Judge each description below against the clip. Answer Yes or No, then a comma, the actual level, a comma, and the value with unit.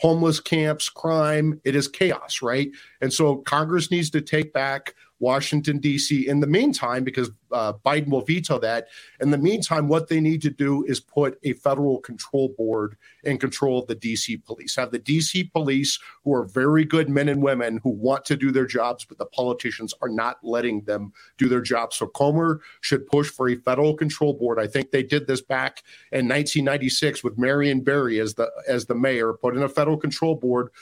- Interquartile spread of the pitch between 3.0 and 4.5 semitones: Yes, average, 3.3 semitones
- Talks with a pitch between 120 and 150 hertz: Yes, medium, 140 Hz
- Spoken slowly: No, average, 200 wpm